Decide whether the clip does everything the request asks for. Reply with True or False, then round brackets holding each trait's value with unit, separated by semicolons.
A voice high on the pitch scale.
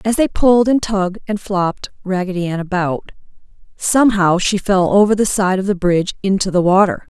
True (195 Hz)